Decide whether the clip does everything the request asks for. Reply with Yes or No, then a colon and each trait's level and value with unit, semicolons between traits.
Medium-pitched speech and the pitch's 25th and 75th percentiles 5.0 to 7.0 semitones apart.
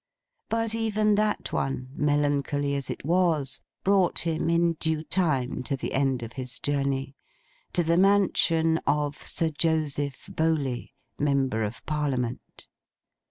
No: medium, 150 Hz; average, 3.6 semitones